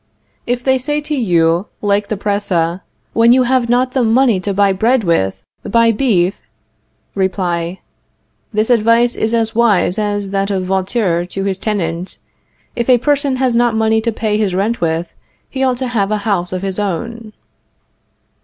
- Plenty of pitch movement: No, average, 4.0 semitones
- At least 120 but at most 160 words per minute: No, average, 170 wpm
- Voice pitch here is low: No, high, 210 Hz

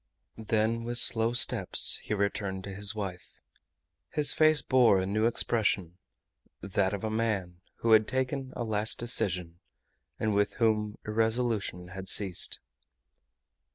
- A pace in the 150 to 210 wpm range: No, slow, 135 wpm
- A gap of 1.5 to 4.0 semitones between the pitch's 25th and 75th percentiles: Yes, average, 3.1 semitones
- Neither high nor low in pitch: No, low, 105 Hz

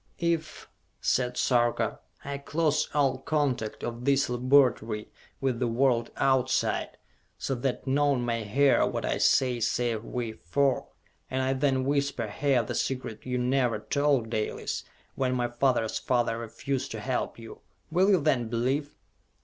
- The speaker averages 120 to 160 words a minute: Yes, average, 150 wpm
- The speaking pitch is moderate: No, low, 130 Hz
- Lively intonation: No, average, 2.8 semitones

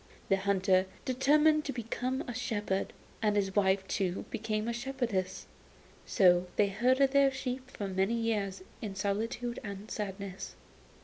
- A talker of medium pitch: No, high, 210 Hz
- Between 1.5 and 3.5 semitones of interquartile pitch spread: No, average, 4.4 semitones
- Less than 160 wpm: Yes, average, 140 wpm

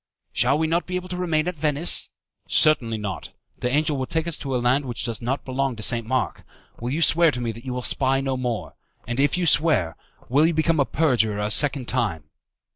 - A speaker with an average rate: No, fast, 230 wpm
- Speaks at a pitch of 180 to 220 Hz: No, low, 135 Hz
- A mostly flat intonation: No, average, 4.5 semitones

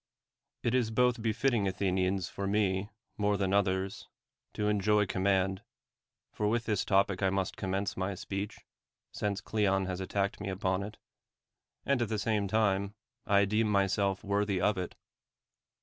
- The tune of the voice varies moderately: No, narrow, 1.7 semitones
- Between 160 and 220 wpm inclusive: No, average, 150 wpm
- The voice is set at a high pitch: No, low, 100 Hz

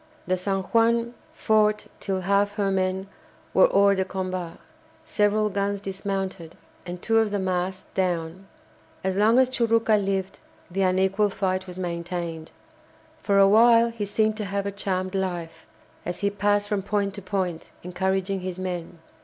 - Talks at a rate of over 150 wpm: Yes, average, 160 wpm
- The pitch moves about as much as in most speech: No, narrow, 1.8 semitones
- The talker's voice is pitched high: Yes, high, 195 Hz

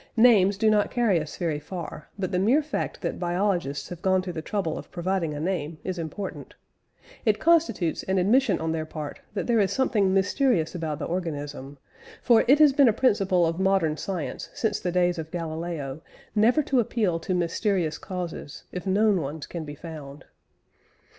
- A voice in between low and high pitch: Yes, medium, 180 Hz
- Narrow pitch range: No, average, 4.3 semitones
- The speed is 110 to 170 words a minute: No, average, 185 wpm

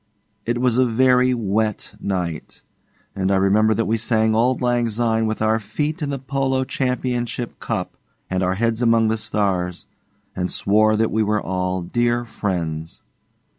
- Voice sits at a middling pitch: No, low, 110 Hz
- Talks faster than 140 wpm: Yes, average, 165 wpm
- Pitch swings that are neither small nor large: Yes, average, 3.5 semitones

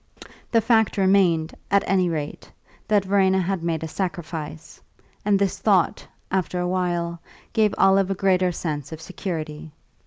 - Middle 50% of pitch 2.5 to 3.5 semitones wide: Yes, average, 3.1 semitones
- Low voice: No, medium, 180 Hz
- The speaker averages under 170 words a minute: Yes, average, 150 wpm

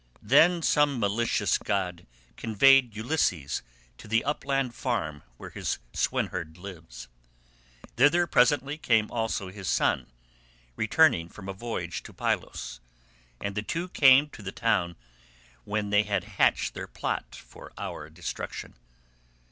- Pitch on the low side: Yes, low, 105 Hz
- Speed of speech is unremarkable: No, slow, 130 wpm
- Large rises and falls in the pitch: Yes, wide, 6.7 semitones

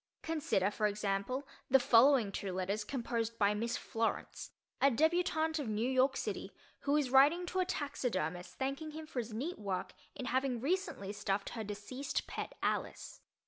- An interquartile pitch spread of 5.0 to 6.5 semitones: Yes, wide, 5.6 semitones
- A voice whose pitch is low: No, very high, 250 Hz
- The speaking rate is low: No, average, 165 wpm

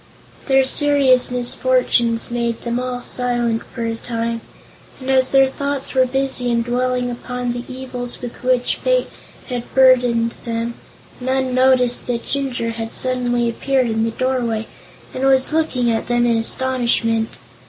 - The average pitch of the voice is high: Yes, high, 245 Hz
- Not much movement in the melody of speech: Yes, narrow, 1.8 semitones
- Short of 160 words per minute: Yes, average, 150 wpm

